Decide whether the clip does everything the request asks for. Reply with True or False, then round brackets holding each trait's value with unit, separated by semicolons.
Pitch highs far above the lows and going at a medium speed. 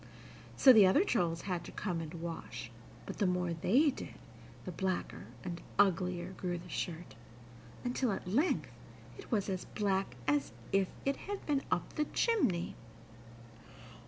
False (4.8 semitones; 155 wpm)